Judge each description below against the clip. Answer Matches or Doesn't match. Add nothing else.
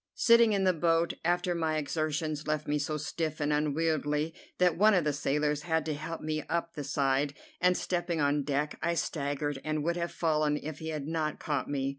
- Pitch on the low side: Doesn't match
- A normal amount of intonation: Doesn't match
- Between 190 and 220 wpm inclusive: Matches